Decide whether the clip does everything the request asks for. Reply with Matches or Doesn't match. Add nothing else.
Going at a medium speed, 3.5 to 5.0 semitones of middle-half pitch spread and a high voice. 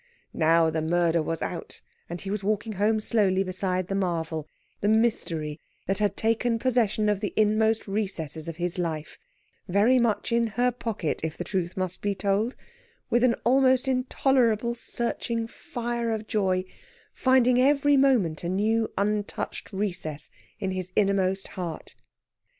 Matches